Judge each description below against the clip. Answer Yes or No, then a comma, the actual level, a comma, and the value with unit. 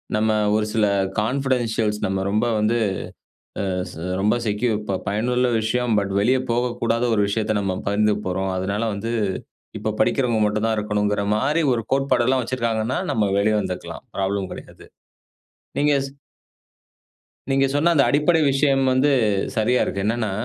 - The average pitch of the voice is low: Yes, low, 110 Hz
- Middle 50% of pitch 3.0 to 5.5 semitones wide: Yes, average, 3.4 semitones